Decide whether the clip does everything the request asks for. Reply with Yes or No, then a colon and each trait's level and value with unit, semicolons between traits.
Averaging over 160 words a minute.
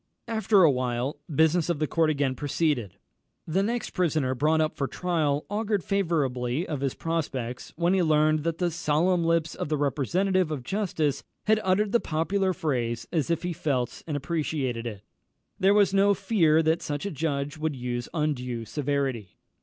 Yes: average, 175 wpm